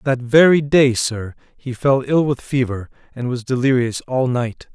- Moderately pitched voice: No, low, 130 Hz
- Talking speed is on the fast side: No, average, 175 wpm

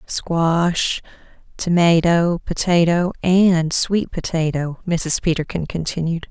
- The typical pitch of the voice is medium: Yes, medium, 170 Hz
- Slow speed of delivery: Yes, slow, 85 wpm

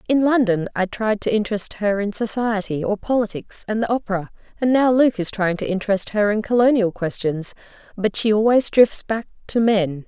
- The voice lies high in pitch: Yes, high, 210 Hz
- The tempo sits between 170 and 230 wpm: Yes, average, 175 wpm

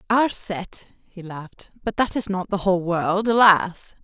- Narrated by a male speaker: No, female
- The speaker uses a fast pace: No, average, 180 wpm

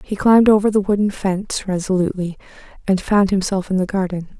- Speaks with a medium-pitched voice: No, high, 195 Hz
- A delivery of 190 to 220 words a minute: No, average, 175 wpm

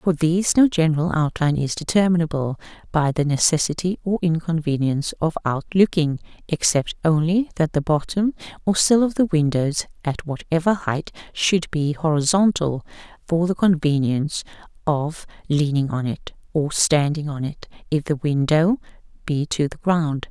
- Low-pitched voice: No, medium, 160 Hz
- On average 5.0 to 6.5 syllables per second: No, 4.8 syllables/s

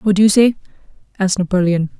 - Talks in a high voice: Yes, high, 195 Hz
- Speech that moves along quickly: No, average, 180 wpm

